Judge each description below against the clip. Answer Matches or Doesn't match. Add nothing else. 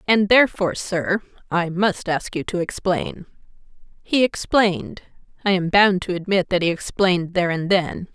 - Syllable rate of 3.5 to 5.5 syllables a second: Matches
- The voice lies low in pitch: Doesn't match